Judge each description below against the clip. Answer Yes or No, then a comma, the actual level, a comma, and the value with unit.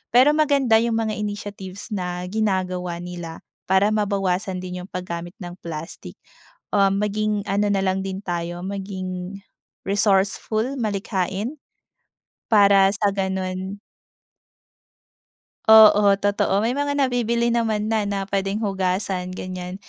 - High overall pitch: Yes, high, 195 Hz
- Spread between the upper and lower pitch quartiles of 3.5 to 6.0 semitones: No, narrow, 2.4 semitones